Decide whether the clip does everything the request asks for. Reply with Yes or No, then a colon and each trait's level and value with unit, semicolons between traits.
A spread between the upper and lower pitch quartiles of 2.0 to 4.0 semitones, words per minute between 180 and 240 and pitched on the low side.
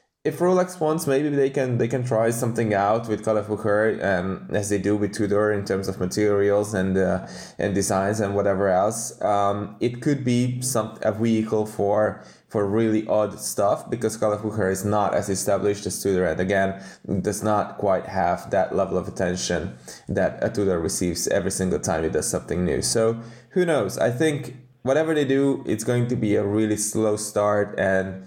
Yes: average, 3.1 semitones; average, 190 wpm; low, 105 Hz